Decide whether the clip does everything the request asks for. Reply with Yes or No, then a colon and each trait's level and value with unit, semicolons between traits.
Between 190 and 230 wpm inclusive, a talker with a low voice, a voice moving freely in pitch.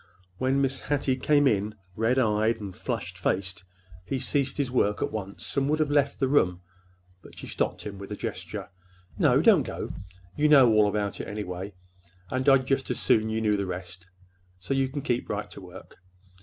Yes: average, 195 wpm; low, 110 Hz; wide, 5.7 semitones